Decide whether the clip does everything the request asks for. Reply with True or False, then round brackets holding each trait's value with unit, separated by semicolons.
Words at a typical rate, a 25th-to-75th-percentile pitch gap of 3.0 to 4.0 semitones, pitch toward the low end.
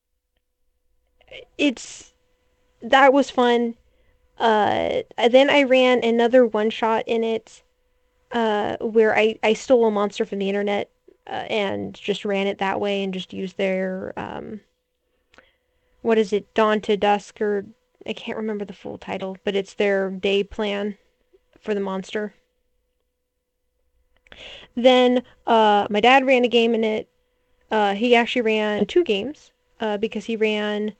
False (145 wpm; 3.6 semitones; 220 Hz)